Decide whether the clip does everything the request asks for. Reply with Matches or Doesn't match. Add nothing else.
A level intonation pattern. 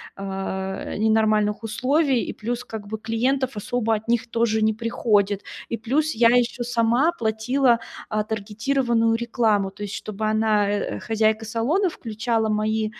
Matches